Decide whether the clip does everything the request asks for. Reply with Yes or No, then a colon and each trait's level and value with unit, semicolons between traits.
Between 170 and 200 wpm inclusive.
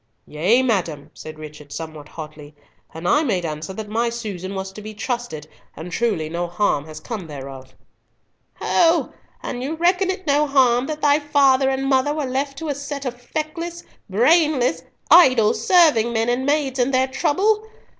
Yes: average, 175 wpm